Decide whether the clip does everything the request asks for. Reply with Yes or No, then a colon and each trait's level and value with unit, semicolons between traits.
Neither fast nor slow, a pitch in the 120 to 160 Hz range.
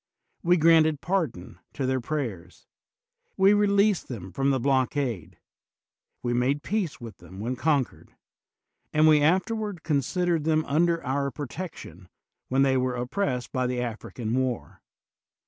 Yes: average, 145 wpm; medium, 140 Hz